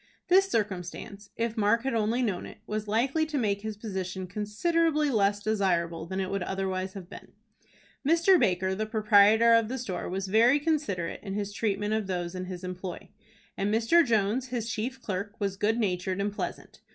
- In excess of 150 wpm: Yes, average, 185 wpm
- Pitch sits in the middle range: No, high, 210 Hz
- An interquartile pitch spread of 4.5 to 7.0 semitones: No, average, 3.5 semitones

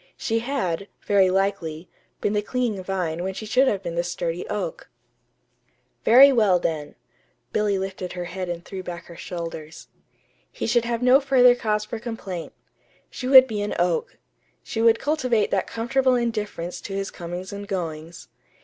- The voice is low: No, high, 200 Hz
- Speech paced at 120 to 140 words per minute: No, average, 165 wpm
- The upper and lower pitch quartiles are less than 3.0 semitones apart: No, average, 5.0 semitones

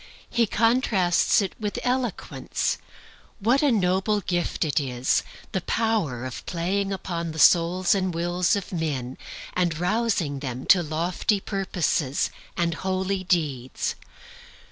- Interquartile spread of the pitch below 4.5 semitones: Yes, average, 3.7 semitones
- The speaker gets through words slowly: Yes, slow, 130 wpm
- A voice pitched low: No, medium, 180 Hz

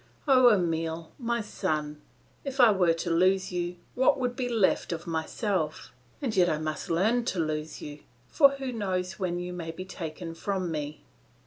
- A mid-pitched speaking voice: Yes, medium, 180 Hz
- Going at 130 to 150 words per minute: No, average, 180 wpm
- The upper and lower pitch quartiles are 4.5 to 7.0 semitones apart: Yes, average, 5.1 semitones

